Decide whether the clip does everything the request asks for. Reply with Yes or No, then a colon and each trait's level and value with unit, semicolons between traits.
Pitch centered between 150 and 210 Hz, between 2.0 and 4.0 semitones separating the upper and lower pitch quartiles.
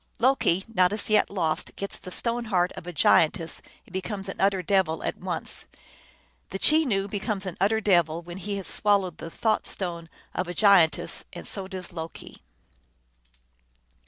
Yes: high, 190 Hz; average, 2.8 semitones